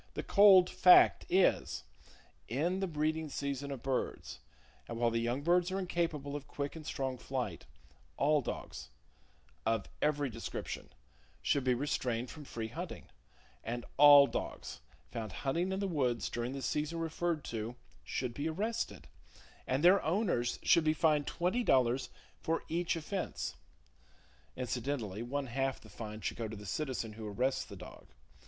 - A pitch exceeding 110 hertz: Yes, medium, 140 Hz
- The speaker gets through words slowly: No, average, 155 wpm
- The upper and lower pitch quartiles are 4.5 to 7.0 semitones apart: Yes, wide, 5.4 semitones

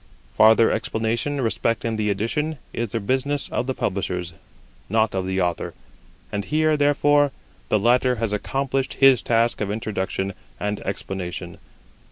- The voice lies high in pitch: No, low, 115 Hz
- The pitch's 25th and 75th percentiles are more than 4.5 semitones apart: Yes, average, 5.0 semitones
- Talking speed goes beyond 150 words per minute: No, average, 140 wpm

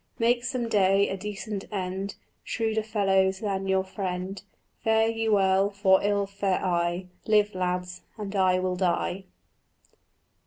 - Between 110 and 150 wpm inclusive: Yes, average, 140 wpm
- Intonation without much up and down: Yes, narrow, 2.0 semitones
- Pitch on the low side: No, high, 195 Hz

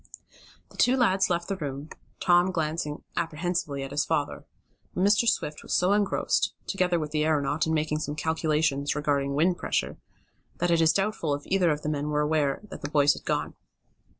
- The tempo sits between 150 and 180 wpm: No, average, 190 wpm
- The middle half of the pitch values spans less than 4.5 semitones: Yes, average, 3.3 semitones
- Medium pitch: Yes, medium, 155 Hz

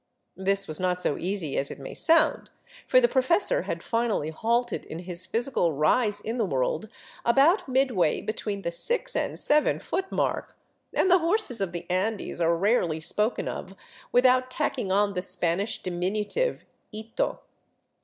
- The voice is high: Yes, high, 210 Hz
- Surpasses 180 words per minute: No, average, 160 wpm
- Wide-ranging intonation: Yes, wide, 6.3 semitones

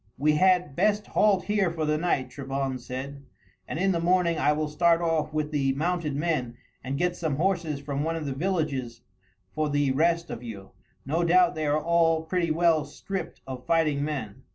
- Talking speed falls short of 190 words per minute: No, average, 195 wpm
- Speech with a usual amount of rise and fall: Yes, average, 3.5 semitones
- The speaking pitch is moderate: Yes, medium, 155 Hz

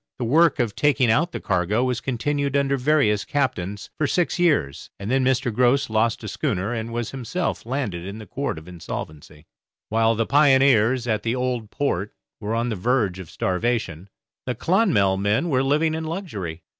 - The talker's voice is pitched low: Yes, low, 120 Hz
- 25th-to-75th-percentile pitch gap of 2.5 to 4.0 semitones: No, average, 5.2 semitones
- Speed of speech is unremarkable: Yes, average, 180 wpm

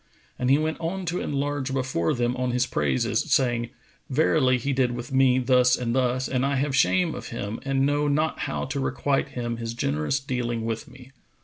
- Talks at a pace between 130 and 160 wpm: No, average, 200 wpm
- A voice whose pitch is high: No, low, 130 Hz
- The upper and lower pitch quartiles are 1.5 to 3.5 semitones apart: Yes, narrow, 2.5 semitones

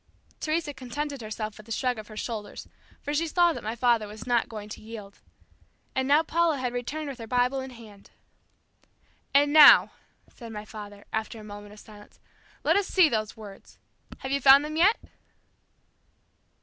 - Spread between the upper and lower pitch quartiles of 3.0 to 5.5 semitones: Yes, average, 5.2 semitones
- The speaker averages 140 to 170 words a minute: No, average, 180 wpm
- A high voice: Yes, high, 240 Hz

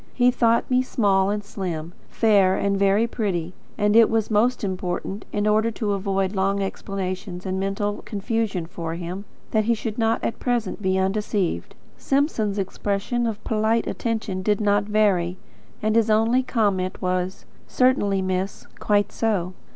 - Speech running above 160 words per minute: No, average, 155 wpm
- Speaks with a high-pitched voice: Yes, high, 205 Hz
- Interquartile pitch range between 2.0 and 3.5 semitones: Yes, average, 2.8 semitones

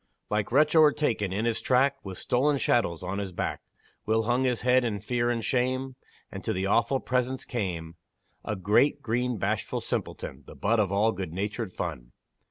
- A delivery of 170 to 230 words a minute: Yes, average, 180 wpm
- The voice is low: Yes, low, 115 Hz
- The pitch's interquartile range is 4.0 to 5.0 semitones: Yes, average, 4.5 semitones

